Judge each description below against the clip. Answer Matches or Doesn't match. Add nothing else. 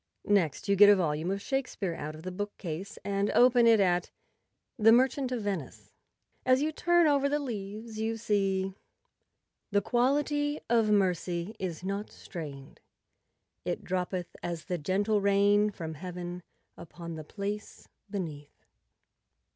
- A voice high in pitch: Matches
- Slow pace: Doesn't match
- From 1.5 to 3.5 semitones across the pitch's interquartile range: Doesn't match